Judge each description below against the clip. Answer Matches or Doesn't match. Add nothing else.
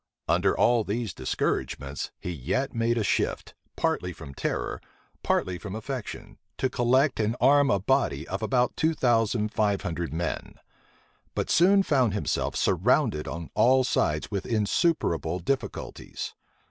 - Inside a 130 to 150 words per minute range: Matches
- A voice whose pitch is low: Matches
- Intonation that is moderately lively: Doesn't match